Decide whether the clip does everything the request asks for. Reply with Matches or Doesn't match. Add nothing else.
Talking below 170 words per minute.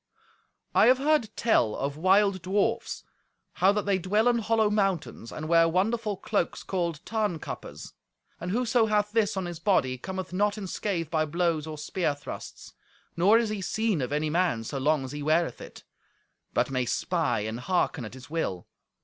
Doesn't match